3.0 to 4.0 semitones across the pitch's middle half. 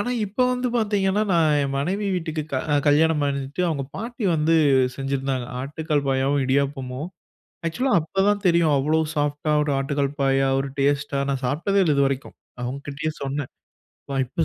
Yes: average, 3.5 semitones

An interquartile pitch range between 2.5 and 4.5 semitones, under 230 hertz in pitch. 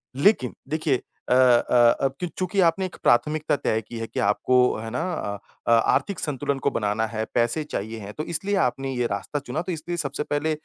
No: average, 5.0 semitones; low, 135 Hz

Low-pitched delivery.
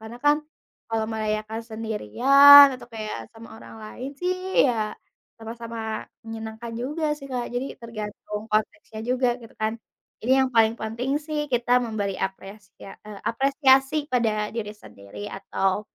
No: high, 225 Hz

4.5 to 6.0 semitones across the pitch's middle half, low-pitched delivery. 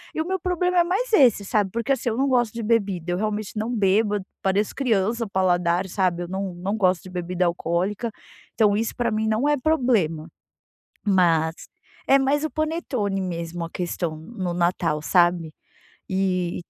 No: average, 5.1 semitones; high, 200 Hz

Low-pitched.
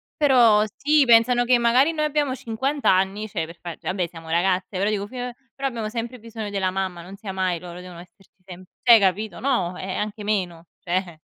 No: high, 205 Hz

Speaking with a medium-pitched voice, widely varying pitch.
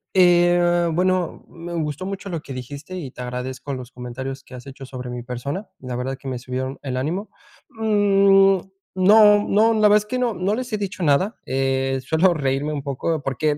Yes: medium, 155 Hz; wide, 6.5 semitones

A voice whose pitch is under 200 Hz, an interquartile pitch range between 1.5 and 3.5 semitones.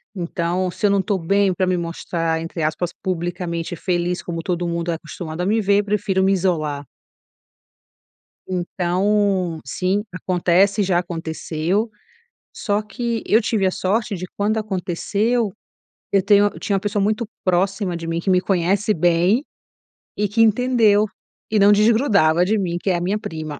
Yes: medium, 185 Hz; average, 3.1 semitones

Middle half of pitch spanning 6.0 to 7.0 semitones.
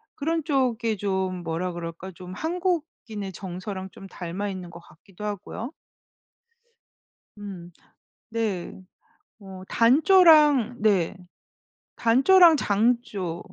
No: wide, 5.6 semitones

